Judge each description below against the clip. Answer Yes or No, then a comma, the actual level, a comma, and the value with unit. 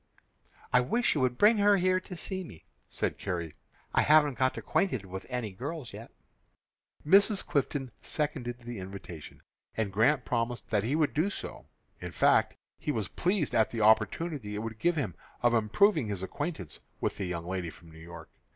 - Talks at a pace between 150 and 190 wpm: Yes, average, 180 wpm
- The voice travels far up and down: Yes, wide, 7.6 semitones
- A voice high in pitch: No, low, 125 Hz